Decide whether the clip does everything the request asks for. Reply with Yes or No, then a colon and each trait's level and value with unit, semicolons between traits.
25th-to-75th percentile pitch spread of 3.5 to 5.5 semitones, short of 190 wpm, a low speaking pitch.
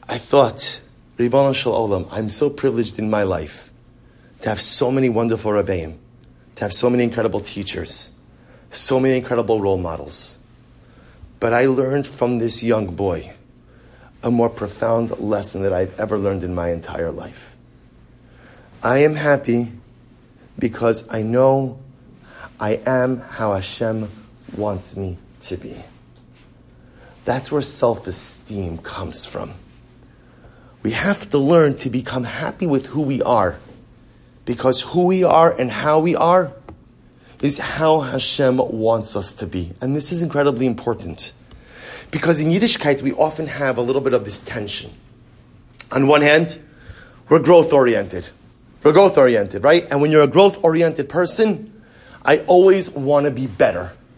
Yes: average, 4.5 semitones; average, 145 wpm; low, 125 Hz